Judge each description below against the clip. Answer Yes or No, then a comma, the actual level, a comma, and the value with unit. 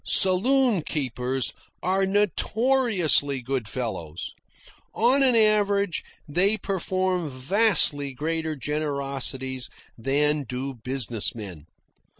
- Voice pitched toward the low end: No, medium, 150 Hz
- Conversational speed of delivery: No, slow, 90 wpm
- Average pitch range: No, wide, 7.3 semitones